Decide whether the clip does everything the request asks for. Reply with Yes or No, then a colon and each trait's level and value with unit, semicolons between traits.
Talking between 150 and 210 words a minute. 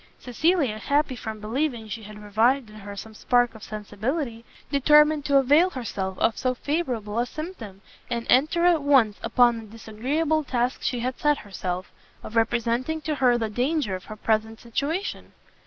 Yes: average, 170 wpm